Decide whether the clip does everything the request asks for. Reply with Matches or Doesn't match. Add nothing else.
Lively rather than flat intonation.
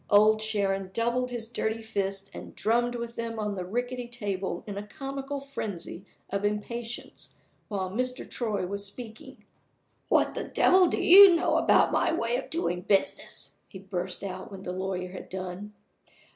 Doesn't match